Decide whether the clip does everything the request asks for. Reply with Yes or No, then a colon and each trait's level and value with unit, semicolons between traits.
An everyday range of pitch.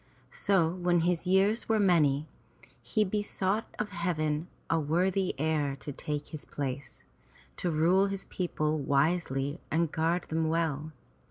Yes: average, 3.5 semitones